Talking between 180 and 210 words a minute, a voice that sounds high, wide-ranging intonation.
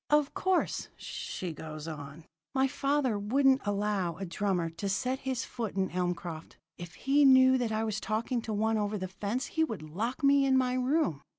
Yes: average, 190 wpm; high, 215 Hz; wide, 6.3 semitones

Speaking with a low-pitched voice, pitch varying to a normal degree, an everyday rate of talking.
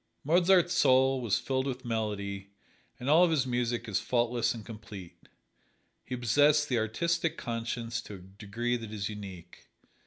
Yes: low, 120 Hz; average, 3.8 semitones; average, 155 wpm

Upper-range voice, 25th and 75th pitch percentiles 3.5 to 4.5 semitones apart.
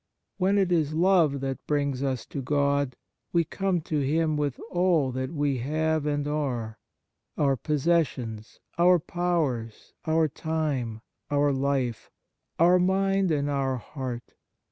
No: medium, 145 Hz; average, 3.8 semitones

